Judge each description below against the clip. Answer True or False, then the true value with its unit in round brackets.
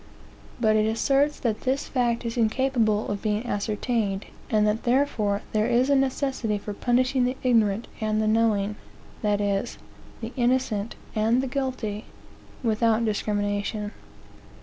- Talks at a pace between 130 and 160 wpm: True (140 wpm)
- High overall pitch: True (225 Hz)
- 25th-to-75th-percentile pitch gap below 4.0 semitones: True (3.0 semitones)